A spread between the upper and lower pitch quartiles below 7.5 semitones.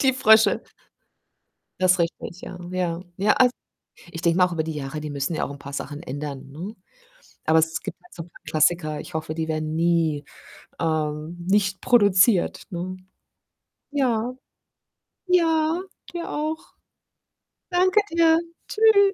No: wide, 8.1 semitones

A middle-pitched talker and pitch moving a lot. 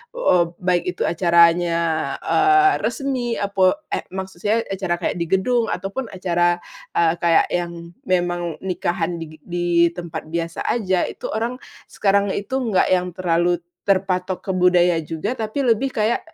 No: medium, 180 Hz; average, 3.2 semitones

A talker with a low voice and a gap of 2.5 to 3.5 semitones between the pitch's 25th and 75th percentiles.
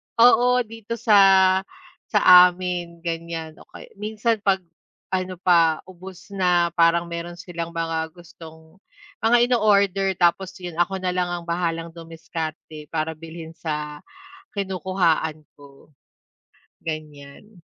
No: medium, 170 Hz; average, 2.8 semitones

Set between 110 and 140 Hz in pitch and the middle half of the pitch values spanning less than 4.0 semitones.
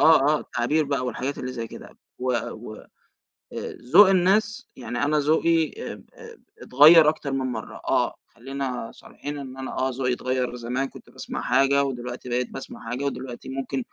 Yes: low, 135 Hz; average, 2.8 semitones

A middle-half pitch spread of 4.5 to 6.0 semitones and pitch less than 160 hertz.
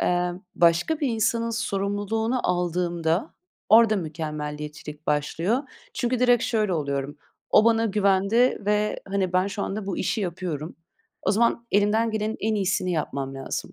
No: average, 4.8 semitones; high, 195 Hz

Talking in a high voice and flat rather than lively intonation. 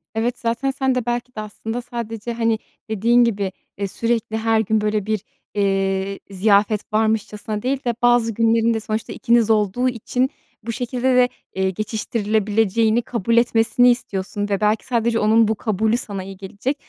Yes: high, 225 Hz; narrow, 2.2 semitones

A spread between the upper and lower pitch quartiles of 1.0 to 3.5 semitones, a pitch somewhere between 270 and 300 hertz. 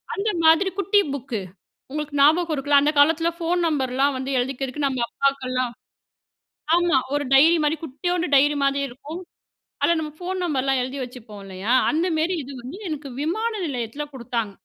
No: average, 4.0 semitones; very high, 285 Hz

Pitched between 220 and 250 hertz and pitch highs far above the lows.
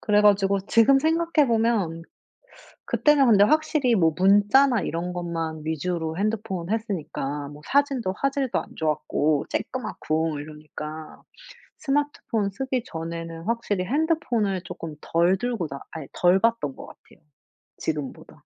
No: high, 195 Hz; wide, 6.9 semitones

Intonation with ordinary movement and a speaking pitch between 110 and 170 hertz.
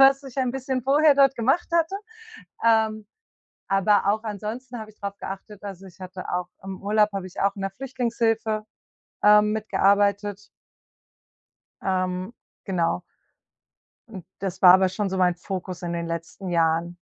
No: average, 3.6 semitones; high, 200 Hz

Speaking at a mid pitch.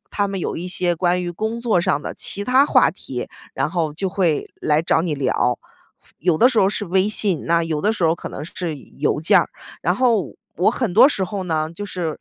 Yes: medium, 180 Hz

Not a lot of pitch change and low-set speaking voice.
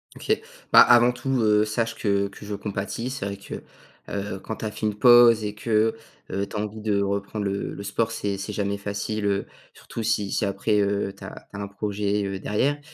Yes: narrow, 1.7 semitones; low, 105 Hz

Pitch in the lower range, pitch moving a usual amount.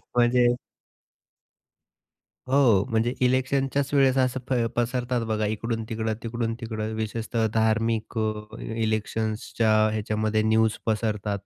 No: low, 110 Hz; narrow, 1.9 semitones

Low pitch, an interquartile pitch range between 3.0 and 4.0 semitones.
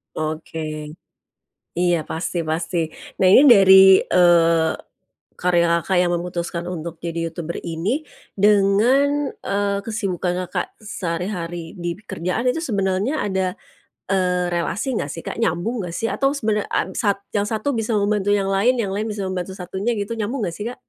No: high, 190 Hz; average, 3.6 semitones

